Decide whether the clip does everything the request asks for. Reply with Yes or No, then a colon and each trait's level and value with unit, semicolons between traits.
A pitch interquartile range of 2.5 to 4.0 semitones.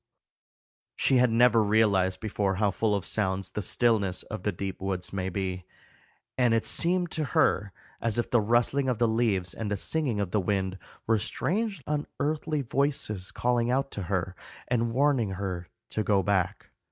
No: average, 4.4 semitones